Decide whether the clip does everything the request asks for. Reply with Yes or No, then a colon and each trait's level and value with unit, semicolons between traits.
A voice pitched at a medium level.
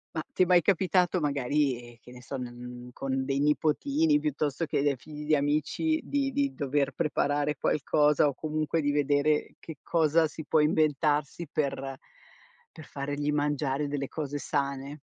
Yes: medium, 150 Hz